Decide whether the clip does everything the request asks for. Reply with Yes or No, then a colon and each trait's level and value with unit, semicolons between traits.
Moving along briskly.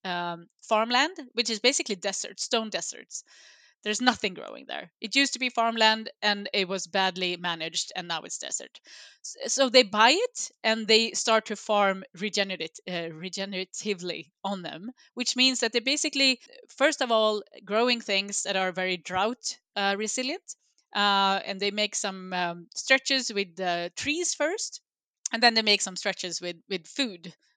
No: average, 165 wpm